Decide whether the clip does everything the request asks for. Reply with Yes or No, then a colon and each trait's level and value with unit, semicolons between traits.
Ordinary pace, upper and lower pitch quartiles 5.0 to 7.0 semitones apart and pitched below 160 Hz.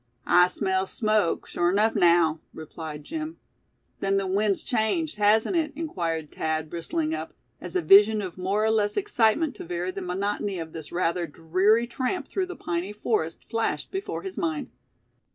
No: average, 170 wpm; wide, 5.5 semitones; high, 200 Hz